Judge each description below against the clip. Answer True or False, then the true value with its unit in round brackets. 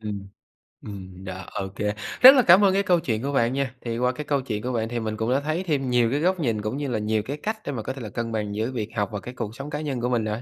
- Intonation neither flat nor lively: True (4.8 semitones)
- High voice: False (120 Hz)